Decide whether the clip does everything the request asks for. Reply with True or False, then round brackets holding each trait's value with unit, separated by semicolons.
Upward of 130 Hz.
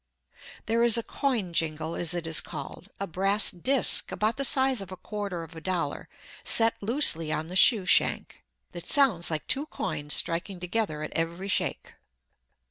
True (185 Hz)